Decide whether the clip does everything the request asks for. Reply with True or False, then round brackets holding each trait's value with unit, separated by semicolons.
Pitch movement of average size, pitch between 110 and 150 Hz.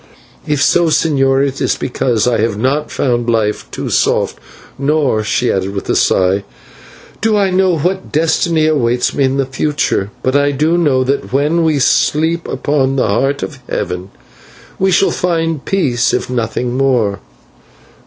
True (4.5 semitones; 135 Hz)